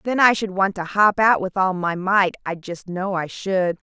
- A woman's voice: Yes, female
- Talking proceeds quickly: Yes, fast, 245 wpm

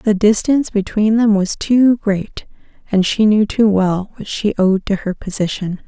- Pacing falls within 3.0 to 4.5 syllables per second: Yes, 4.4 syllables/s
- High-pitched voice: Yes, high, 205 Hz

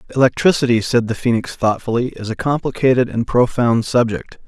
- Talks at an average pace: Yes, average, 145 wpm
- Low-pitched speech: Yes, low, 120 Hz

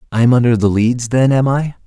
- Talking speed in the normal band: No, fast, 255 wpm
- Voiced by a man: Yes, male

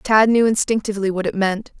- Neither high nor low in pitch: No, high, 210 Hz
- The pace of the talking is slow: No, average, 200 wpm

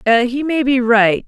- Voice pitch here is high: Yes, very high, 250 Hz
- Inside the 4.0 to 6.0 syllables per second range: No, 3.5 syllables/s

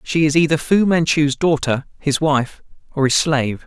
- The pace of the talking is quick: No, average, 180 wpm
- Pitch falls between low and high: Yes, medium, 150 Hz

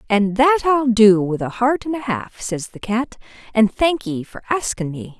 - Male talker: No, female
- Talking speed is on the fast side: Yes, fast, 220 wpm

